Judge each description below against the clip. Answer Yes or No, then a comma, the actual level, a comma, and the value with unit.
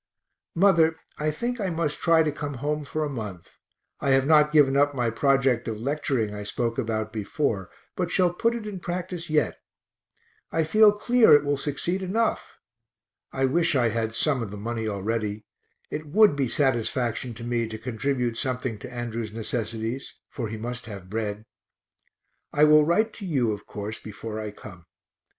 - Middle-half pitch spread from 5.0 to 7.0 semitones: Yes, wide, 5.6 semitones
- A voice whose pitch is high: No, low, 130 Hz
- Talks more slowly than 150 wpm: No, average, 175 wpm